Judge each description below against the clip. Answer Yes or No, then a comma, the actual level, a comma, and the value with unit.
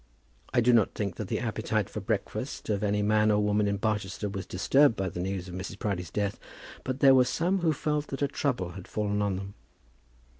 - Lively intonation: No, average, 4.5 semitones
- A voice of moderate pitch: No, low, 105 Hz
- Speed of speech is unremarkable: No, fast, 220 wpm